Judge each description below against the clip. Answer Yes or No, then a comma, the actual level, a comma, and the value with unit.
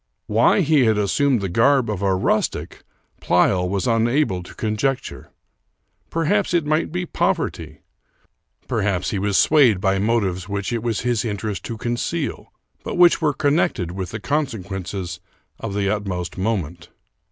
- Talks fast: No, average, 145 wpm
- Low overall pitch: Yes, low, 105 Hz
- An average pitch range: No, wide, 6.1 semitones